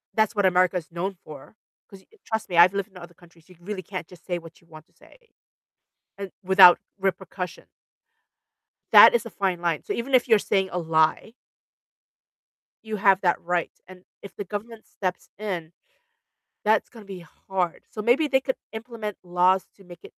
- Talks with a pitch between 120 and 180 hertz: No, high, 190 Hz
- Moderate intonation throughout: Yes, average, 3.1 semitones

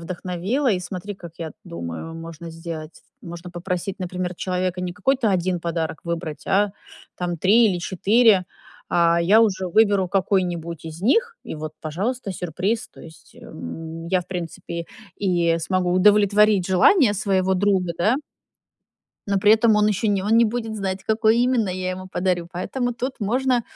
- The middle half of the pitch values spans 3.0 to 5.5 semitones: Yes, average, 3.6 semitones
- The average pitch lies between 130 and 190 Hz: Yes, medium, 185 Hz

